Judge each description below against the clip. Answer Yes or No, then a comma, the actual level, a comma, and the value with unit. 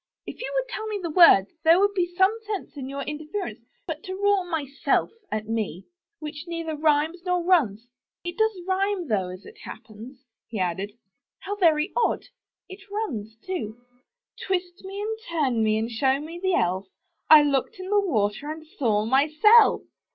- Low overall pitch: No, very high, 320 Hz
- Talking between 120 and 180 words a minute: No, average, 190 wpm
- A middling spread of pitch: No, wide, 7.9 semitones